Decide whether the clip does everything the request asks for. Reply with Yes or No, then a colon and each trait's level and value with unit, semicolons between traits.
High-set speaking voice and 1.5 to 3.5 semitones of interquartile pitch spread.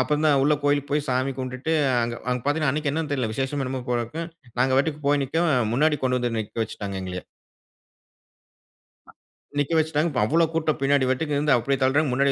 No: medium, 140 Hz; average, 3.0 semitones